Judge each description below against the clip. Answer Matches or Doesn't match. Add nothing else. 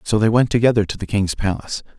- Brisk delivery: Matches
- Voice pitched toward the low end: Matches